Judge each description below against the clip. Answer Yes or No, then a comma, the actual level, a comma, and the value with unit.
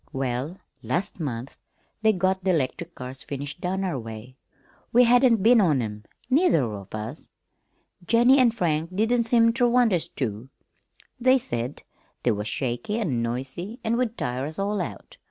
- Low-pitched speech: No, medium, 170 Hz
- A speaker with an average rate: Yes, average, 165 wpm